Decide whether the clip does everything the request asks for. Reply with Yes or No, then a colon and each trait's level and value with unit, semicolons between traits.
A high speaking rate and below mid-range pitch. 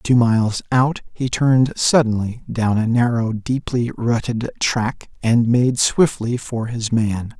No: average, 145 wpm; low, 120 Hz